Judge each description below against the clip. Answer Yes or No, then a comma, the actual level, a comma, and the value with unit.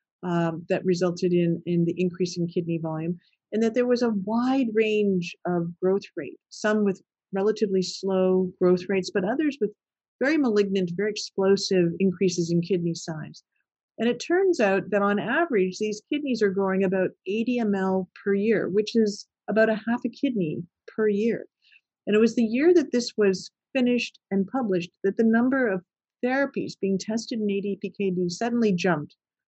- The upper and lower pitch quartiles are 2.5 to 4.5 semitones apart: Yes, average, 3.7 semitones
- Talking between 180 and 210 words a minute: No, average, 170 wpm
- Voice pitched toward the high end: Yes, high, 200 Hz